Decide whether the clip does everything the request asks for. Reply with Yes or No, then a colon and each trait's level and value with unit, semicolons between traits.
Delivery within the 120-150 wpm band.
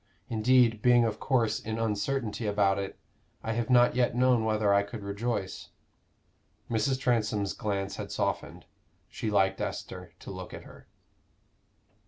Yes: average, 145 wpm